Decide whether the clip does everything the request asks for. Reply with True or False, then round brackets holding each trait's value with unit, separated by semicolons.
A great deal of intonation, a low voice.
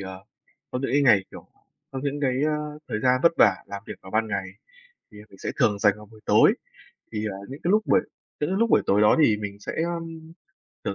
True (6.5 semitones; 115 Hz)